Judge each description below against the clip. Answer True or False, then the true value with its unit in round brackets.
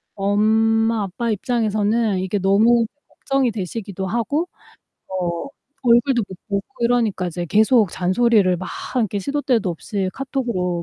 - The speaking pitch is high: True (215 Hz)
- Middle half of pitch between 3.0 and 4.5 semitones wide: True (3.8 semitones)